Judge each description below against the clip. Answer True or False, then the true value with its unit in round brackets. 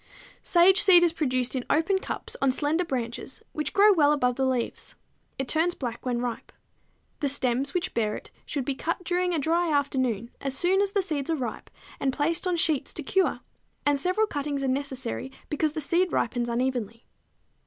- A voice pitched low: False (285 Hz)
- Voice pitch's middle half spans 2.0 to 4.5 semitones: False (5.1 semitones)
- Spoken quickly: False (190 wpm)